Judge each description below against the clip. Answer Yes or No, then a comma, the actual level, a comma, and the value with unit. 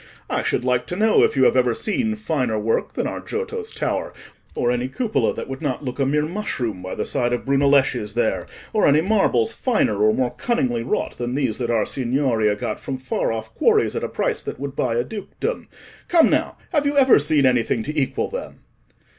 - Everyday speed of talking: No, fast, 215 wpm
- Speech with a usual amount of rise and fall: No, wide, 6.9 semitones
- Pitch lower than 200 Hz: Yes, low, 135 Hz